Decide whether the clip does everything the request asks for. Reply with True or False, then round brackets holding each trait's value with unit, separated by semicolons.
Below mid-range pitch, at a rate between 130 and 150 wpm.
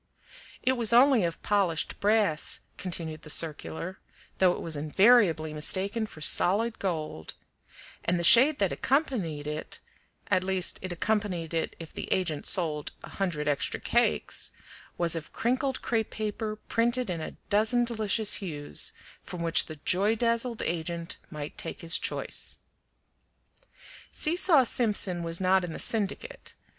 False (190 Hz; 145 wpm)